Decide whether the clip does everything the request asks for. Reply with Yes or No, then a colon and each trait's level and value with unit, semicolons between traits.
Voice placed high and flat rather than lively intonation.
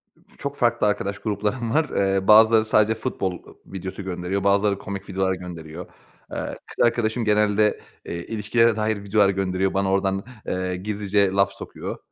No: low, 100 Hz; narrow, 2.2 semitones